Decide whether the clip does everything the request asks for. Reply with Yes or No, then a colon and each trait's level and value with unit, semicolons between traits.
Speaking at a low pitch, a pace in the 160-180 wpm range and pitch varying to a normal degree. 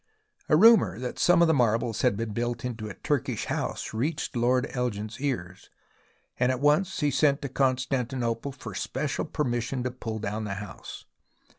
Yes: low, 125 Hz; average, 165 wpm; average, 3.8 semitones